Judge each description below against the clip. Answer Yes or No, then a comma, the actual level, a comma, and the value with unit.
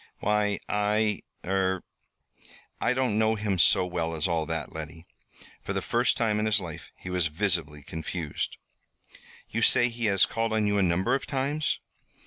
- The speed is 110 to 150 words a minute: No, average, 170 wpm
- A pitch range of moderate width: Yes, average, 4.5 semitones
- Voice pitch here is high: No, low, 100 Hz